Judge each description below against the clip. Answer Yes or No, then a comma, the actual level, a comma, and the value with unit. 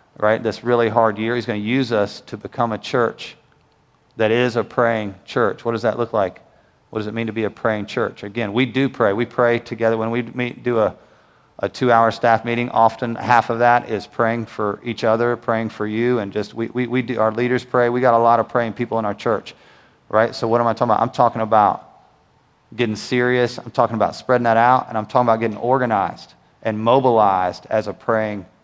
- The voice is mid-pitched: No, low, 115 Hz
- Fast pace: Yes, fast, 230 wpm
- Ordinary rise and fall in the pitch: No, narrow, 1.7 semitones